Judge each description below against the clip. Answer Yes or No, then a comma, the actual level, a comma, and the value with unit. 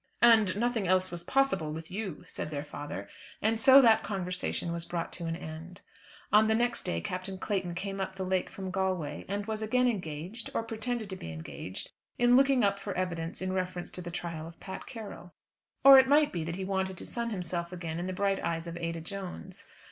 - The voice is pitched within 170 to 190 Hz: Yes, medium, 185 Hz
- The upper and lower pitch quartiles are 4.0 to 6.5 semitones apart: Yes, average, 4.3 semitones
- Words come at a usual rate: No, fast, 215 wpm